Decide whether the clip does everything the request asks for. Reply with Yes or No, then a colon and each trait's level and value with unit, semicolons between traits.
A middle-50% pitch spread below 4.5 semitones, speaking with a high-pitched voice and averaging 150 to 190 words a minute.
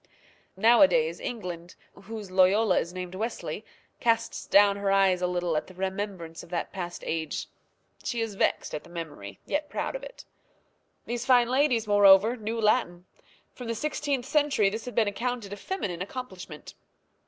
No: average, 4.8 semitones; high, 205 Hz; average, 165 wpm